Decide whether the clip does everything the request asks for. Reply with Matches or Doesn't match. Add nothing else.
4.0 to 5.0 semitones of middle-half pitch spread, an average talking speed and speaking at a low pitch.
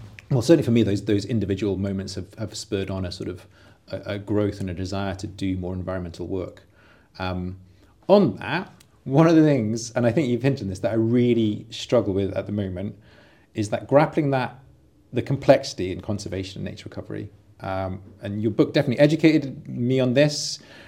Matches